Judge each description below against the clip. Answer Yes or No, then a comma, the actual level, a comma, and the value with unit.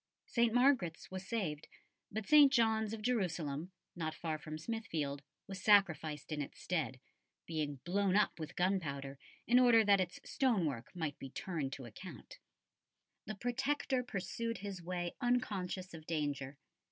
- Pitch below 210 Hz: Yes, medium, 185 Hz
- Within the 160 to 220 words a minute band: No, average, 150 wpm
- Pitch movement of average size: No, wide, 6.2 semitones